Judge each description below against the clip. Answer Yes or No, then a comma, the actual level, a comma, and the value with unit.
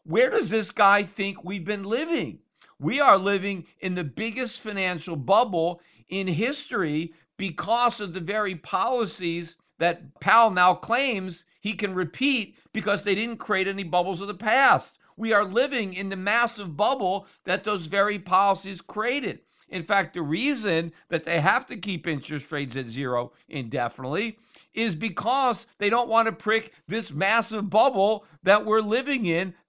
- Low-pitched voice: No, high, 200 Hz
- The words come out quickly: No, average, 160 wpm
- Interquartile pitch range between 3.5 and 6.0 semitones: Yes, average, 4.2 semitones